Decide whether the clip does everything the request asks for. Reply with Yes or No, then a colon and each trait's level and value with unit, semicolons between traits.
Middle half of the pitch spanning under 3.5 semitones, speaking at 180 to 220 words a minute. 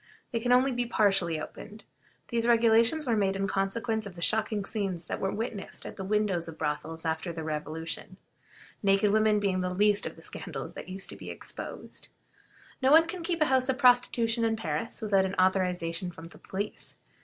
No: average, 4.3 semitones; average, 195 wpm